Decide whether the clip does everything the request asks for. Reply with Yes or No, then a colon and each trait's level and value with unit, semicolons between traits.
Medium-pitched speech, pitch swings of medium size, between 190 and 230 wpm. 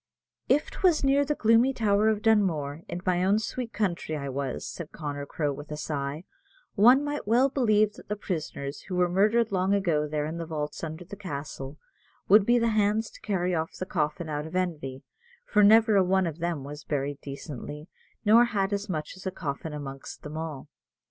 No: medium, 180 Hz; wide, 6.0 semitones; average, 200 wpm